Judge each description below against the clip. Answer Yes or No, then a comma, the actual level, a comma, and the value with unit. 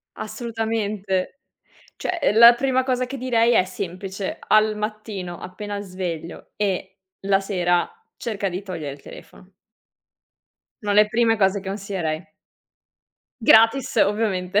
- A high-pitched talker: Yes, high, 205 Hz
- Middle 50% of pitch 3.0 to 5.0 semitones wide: Yes, average, 3.3 semitones